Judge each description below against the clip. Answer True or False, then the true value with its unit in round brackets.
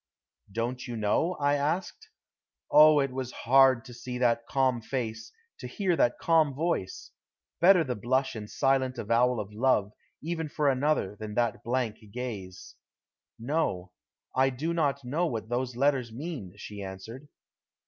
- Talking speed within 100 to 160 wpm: True (150 wpm)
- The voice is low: True (130 Hz)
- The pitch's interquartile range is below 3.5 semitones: False (4.0 semitones)